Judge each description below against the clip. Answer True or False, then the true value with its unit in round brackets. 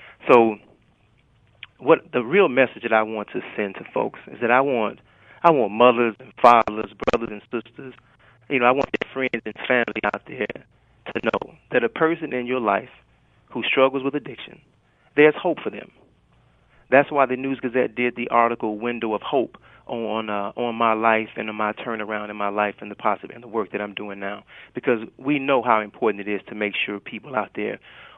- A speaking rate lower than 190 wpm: False (205 wpm)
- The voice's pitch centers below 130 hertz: True (115 Hz)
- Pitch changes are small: False (3.3 semitones)